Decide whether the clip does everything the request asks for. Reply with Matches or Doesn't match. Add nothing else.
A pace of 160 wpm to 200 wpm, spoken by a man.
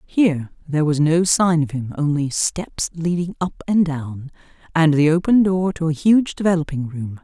Doesn't match